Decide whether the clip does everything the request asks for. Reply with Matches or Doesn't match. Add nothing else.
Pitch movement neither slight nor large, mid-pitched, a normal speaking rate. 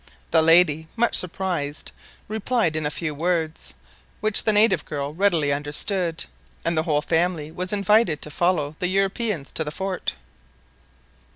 Matches